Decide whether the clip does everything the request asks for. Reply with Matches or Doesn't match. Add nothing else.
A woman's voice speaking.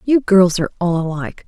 Matches